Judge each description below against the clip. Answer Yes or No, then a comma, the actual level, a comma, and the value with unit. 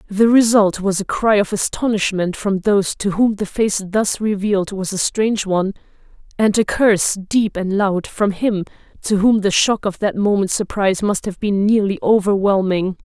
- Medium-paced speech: Yes, average, 185 wpm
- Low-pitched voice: No, high, 200 Hz